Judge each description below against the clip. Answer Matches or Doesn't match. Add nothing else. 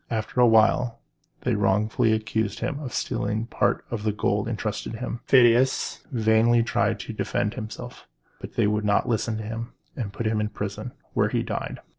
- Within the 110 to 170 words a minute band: Doesn't match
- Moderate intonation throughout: Doesn't match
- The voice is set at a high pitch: Doesn't match